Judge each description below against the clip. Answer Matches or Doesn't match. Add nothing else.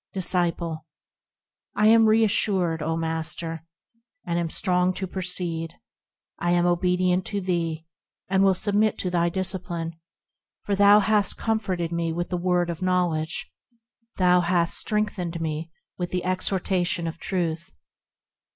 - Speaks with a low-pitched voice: Doesn't match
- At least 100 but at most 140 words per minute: Matches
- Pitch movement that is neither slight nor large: Doesn't match